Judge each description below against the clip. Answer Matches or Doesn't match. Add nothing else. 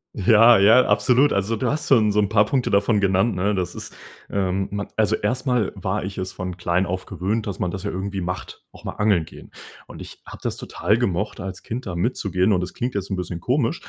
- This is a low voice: Matches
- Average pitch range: Matches